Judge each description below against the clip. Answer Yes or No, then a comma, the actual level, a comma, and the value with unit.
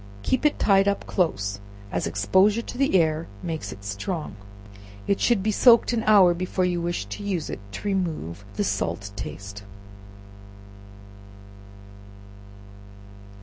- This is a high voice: No, medium, 175 Hz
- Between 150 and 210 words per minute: No, slow, 135 wpm